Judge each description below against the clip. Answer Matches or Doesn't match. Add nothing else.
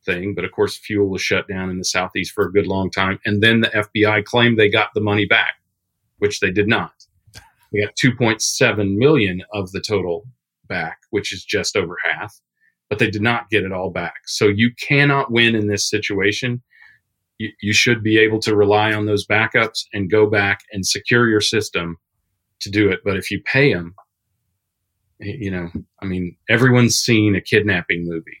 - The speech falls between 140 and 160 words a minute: Doesn't match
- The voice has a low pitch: Matches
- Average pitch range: Doesn't match